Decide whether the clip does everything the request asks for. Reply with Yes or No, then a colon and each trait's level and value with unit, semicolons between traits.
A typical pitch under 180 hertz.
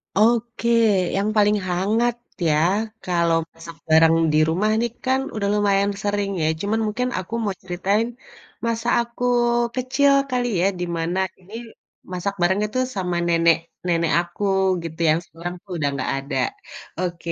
No: high, 195 Hz